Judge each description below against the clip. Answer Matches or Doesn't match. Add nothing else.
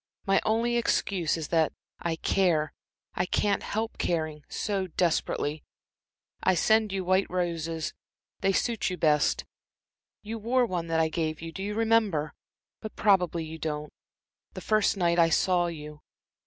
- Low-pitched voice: Doesn't match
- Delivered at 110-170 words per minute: Matches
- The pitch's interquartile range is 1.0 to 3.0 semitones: Doesn't match